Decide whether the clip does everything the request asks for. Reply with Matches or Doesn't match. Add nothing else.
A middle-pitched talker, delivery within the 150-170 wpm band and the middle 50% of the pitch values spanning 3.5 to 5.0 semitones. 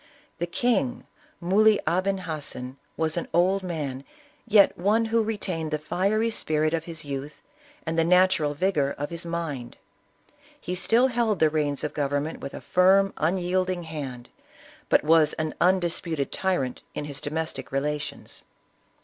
Matches